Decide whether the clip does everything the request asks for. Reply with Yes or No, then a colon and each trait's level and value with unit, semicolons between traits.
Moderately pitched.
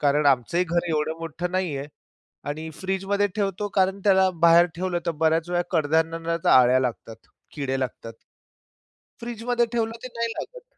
Yes: medium, 170 Hz